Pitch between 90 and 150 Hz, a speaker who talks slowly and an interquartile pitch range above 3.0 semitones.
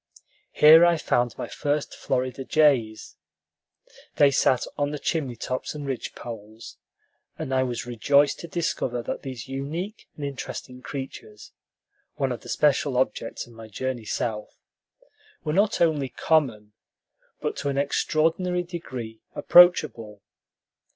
Yes: low, 135 Hz; slow, 130 wpm; average, 4.1 semitones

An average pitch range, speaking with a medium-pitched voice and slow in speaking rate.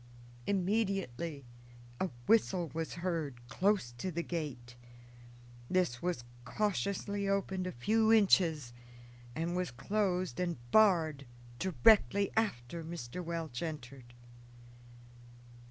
No: wide, 6.0 semitones; medium, 170 Hz; slow, 95 wpm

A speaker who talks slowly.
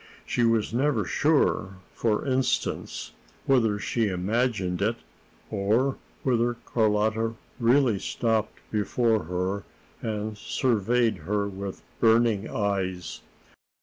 Yes: slow, 100 wpm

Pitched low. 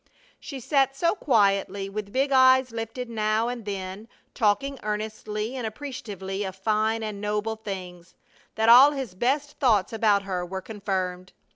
No: high, 215 Hz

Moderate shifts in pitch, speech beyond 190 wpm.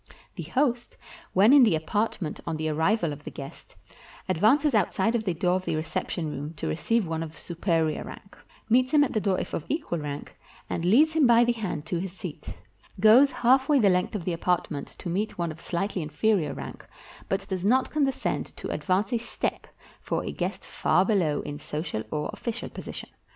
No: wide, 6.2 semitones; average, 200 wpm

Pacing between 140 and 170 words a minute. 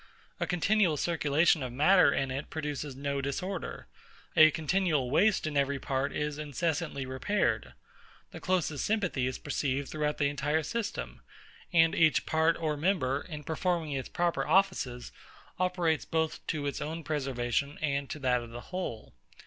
Yes: average, 155 wpm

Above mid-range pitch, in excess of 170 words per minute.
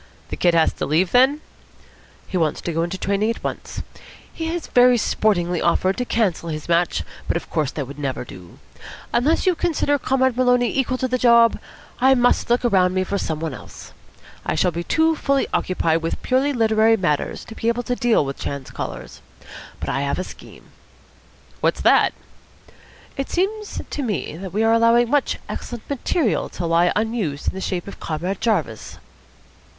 Yes: high, 215 Hz; average, 185 wpm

